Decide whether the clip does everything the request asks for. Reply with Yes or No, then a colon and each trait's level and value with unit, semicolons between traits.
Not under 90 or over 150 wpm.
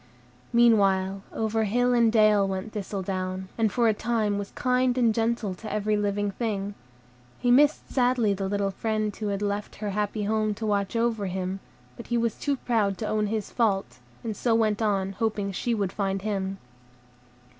No: average, 180 wpm